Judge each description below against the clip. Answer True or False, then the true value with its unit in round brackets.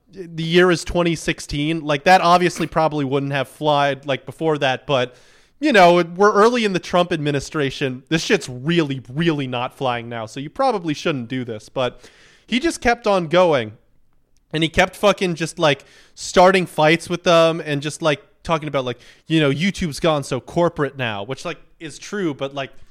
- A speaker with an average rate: True (185 wpm)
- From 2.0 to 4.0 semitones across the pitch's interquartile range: False (4.4 semitones)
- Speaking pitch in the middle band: True (155 Hz)